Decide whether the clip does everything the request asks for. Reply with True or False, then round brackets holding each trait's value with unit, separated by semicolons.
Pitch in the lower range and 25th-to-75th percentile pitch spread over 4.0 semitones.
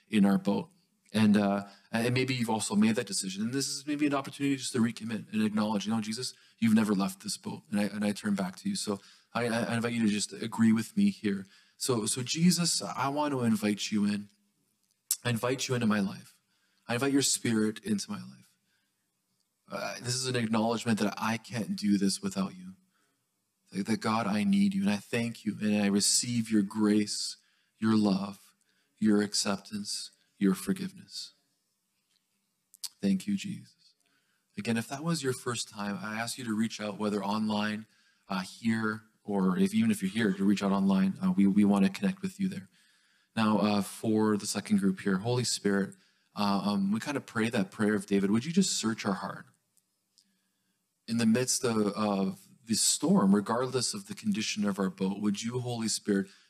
True (110 Hz; 4.4 semitones)